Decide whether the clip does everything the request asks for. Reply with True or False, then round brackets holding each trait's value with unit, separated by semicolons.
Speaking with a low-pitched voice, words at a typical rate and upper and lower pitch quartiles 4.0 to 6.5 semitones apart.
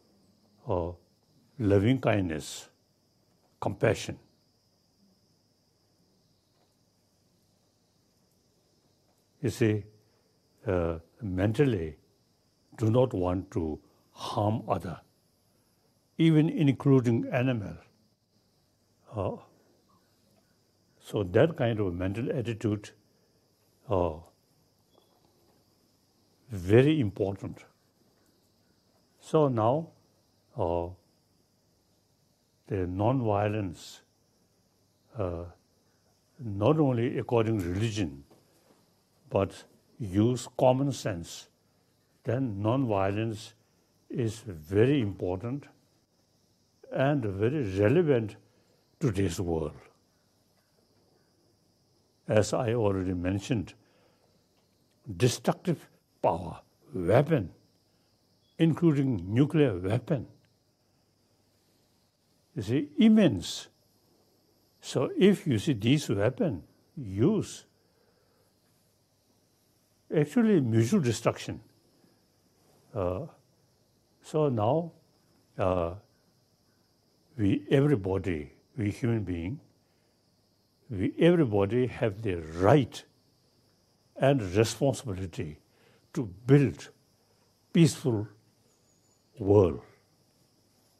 False (110 Hz; 65 wpm; 4.9 semitones)